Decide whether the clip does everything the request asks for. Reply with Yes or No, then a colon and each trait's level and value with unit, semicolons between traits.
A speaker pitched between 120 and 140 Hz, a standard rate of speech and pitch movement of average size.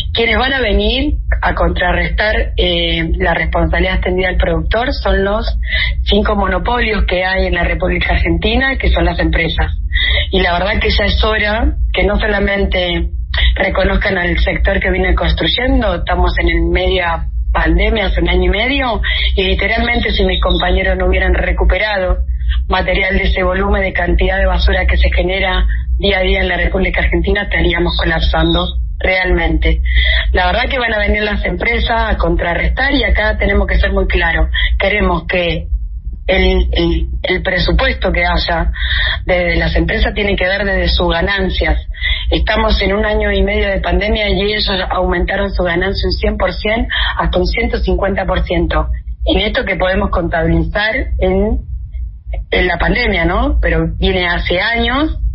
No: medium, 185 Hz; average, 165 wpm; average, 3.8 semitones